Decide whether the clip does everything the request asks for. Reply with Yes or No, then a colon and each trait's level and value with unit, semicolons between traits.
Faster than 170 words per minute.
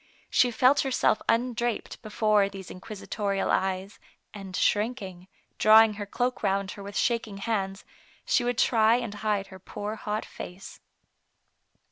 No: average, 145 wpm